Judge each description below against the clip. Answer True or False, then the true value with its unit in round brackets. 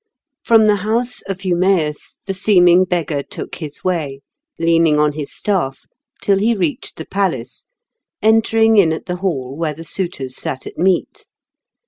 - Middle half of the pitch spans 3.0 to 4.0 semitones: False (4.6 semitones)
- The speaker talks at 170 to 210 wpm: False (155 wpm)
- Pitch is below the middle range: False (175 Hz)